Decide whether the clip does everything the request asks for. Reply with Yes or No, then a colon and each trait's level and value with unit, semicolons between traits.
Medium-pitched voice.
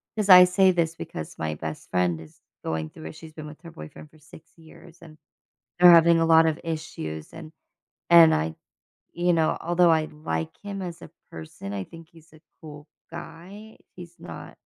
Yes: medium, 160 Hz